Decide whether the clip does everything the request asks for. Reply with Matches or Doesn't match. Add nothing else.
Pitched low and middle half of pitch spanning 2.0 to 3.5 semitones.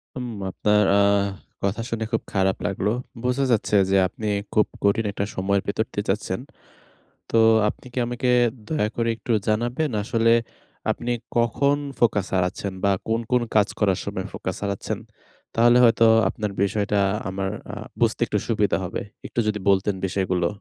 Matches